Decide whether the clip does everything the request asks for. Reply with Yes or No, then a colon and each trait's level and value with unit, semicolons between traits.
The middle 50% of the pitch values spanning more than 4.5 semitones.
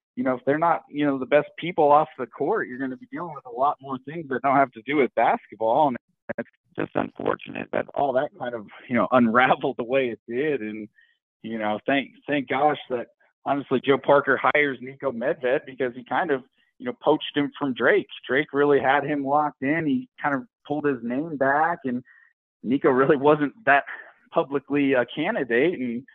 No: narrow, 2.5 semitones